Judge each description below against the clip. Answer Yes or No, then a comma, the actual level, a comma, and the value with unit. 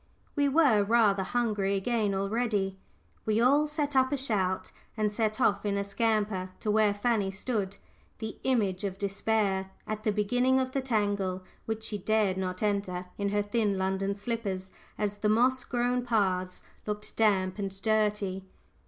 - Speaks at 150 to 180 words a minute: Yes, average, 160 wpm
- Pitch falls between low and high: No, high, 210 Hz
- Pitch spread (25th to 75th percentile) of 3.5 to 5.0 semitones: No, average, 2.9 semitones